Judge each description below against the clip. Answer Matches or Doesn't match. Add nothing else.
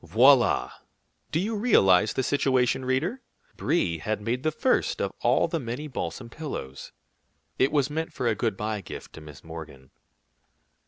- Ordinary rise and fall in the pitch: Doesn't match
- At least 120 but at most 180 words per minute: Matches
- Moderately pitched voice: Doesn't match